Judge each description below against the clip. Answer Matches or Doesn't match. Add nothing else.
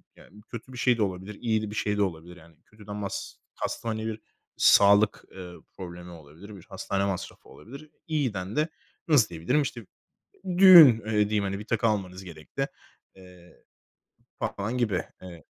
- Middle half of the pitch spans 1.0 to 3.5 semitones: Doesn't match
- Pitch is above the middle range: Doesn't match